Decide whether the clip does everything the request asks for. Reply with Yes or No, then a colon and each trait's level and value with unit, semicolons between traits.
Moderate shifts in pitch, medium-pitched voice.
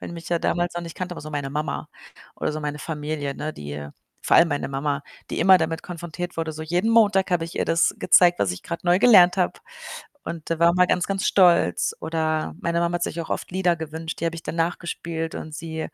No: narrow, 2.1 semitones; medium, 165 Hz